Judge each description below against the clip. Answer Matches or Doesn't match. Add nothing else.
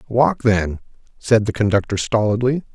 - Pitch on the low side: Matches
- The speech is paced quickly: Doesn't match